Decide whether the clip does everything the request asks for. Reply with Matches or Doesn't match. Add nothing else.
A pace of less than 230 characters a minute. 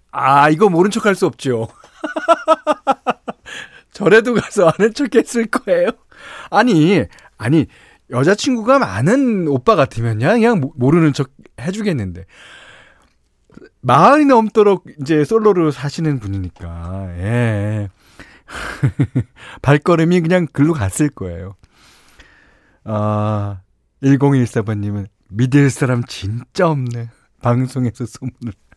Matches